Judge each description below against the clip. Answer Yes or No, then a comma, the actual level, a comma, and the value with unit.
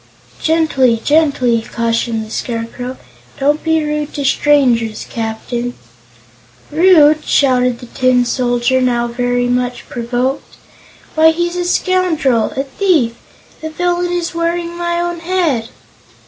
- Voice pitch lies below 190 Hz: No, very high, 270 Hz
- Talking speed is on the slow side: Yes, slow, 120 wpm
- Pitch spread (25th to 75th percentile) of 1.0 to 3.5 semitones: No, average, 5.3 semitones